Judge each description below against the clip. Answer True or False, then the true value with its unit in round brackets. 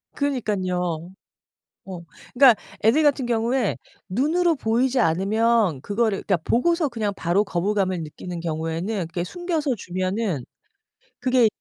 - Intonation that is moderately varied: False (5.9 semitones)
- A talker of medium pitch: False (215 Hz)